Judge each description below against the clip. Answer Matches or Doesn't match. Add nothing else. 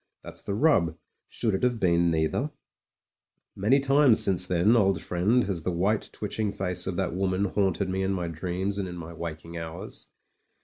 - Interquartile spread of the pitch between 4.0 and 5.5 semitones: Doesn't match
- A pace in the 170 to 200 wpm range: Matches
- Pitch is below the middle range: Matches